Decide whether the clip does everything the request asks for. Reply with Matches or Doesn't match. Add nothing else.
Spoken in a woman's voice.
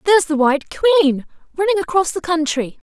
Matches